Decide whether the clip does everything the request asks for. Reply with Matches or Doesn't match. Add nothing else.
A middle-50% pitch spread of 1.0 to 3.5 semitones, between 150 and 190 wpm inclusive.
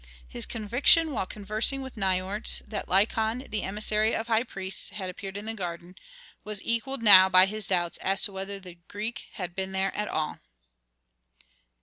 Matches